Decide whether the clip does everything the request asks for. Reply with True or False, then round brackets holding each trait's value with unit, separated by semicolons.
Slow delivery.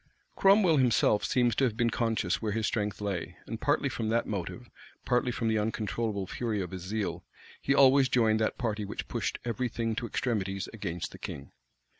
False (190 wpm)